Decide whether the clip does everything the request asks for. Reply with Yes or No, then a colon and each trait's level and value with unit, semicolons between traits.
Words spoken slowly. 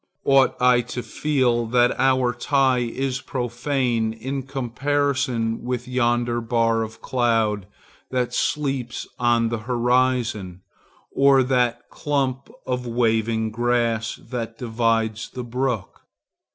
Yes: slow, 110 wpm